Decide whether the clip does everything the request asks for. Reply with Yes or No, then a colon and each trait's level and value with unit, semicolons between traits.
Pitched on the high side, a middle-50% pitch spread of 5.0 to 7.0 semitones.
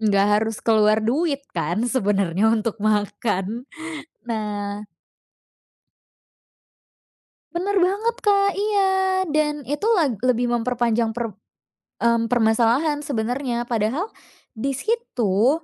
Yes: high, 235 Hz; wide, 5.4 semitones